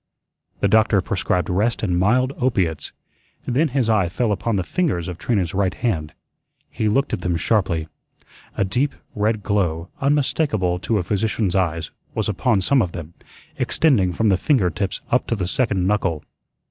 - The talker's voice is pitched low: Yes, low, 100 Hz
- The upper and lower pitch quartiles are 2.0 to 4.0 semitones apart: No, average, 4.5 semitones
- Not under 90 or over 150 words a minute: No, average, 170 wpm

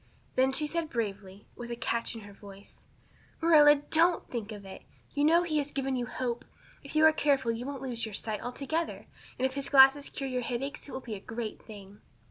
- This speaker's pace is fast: Yes, fast, 225 wpm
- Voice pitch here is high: Yes, very high, 260 Hz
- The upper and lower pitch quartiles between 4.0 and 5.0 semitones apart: Yes, average, 4.3 semitones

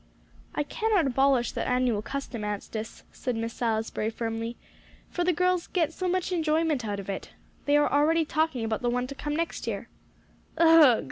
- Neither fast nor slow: Yes, average, 180 wpm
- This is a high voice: Yes, very high, 275 Hz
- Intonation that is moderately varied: No, wide, 6.2 semitones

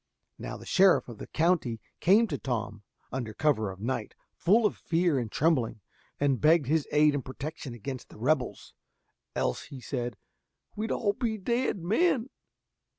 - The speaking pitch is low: No, medium, 150 Hz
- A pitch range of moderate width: No, wide, 6.7 semitones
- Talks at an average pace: Yes, average, 160 wpm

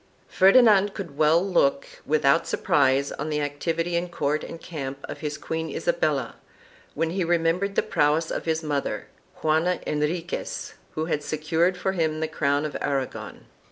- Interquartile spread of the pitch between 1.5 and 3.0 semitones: Yes, narrow, 2.6 semitones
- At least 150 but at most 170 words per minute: Yes, average, 160 wpm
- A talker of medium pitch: Yes, medium, 160 Hz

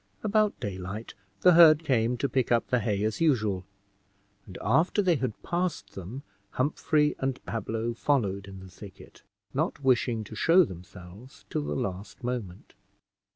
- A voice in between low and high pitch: No, low, 115 Hz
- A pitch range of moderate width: No, wide, 6.3 semitones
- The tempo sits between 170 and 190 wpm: No, average, 155 wpm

